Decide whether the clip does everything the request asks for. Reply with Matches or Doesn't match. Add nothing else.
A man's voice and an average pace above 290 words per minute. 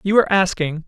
Doesn't match